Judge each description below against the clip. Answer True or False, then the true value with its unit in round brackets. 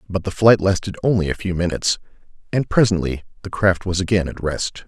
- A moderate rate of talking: True (195 wpm)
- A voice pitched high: False (95 Hz)